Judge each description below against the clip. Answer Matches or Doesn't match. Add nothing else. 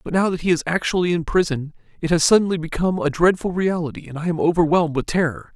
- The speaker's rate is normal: Doesn't match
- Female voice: Doesn't match